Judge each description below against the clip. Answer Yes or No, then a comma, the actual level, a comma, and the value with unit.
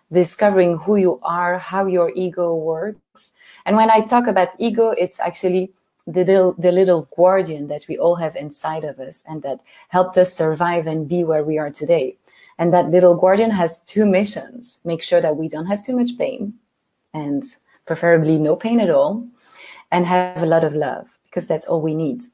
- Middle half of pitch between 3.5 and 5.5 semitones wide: Yes, average, 4.4 semitones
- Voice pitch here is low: No, medium, 180 Hz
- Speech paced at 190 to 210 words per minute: Yes, average, 195 wpm